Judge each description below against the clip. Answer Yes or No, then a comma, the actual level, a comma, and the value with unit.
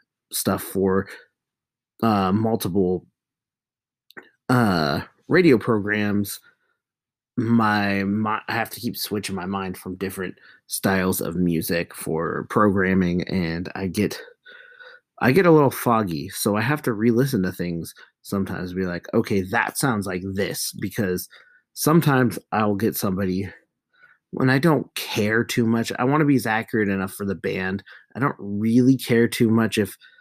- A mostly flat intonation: No, average, 3.8 semitones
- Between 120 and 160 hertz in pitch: No, low, 105 Hz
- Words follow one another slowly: No, average, 145 wpm